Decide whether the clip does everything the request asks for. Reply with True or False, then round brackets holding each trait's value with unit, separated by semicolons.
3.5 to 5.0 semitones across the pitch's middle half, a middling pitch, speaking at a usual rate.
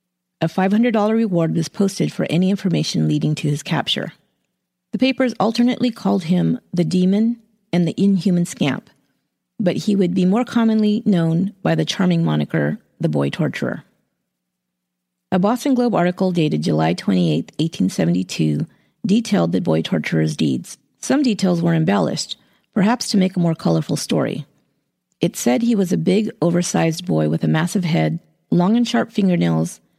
False (5.4 semitones; 180 Hz; 155 wpm)